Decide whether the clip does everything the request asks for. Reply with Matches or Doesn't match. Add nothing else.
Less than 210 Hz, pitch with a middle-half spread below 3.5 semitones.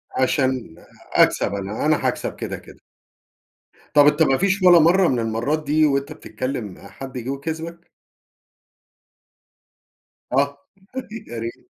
Doesn't match